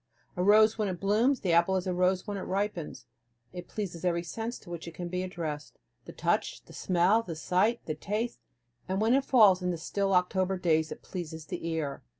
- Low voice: No, medium, 185 Hz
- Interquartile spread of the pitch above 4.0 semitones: No, average, 3.3 semitones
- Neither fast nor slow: No, fast, 215 wpm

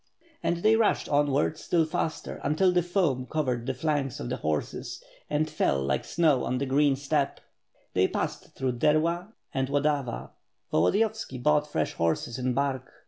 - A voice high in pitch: No, medium, 145 Hz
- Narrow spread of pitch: No, average, 3.6 semitones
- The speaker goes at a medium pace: Yes, average, 165 wpm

